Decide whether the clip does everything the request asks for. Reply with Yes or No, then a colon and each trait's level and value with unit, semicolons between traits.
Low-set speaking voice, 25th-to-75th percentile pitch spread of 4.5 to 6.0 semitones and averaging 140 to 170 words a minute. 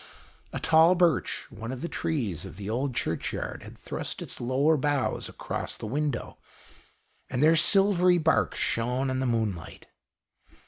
Yes: low, 130 Hz; wide, 5.6 semitones; average, 150 wpm